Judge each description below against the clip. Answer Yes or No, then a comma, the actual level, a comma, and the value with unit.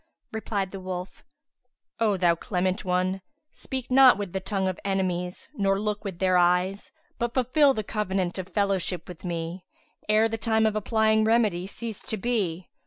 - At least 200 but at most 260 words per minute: No, average, 170 wpm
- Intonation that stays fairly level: No, average, 3.2 semitones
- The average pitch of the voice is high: Yes, high, 195 Hz